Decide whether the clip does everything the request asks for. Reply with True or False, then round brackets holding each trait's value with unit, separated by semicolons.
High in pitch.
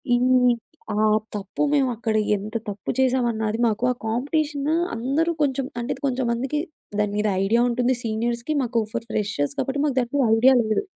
True (240 Hz)